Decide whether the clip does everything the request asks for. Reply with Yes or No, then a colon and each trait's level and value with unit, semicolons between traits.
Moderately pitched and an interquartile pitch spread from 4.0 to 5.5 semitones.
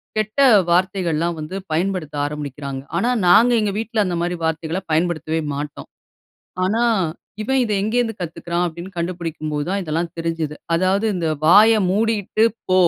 Yes: medium, 175 Hz; average, 4.4 semitones